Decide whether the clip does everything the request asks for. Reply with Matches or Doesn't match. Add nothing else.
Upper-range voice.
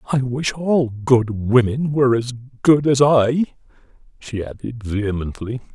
Doesn't match